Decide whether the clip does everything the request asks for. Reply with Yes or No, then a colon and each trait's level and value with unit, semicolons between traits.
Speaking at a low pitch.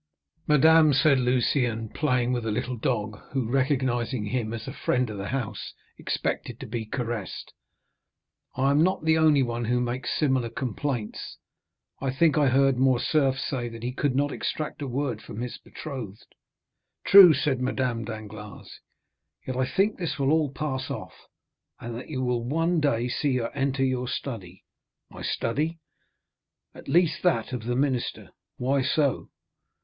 Yes: low, 130 Hz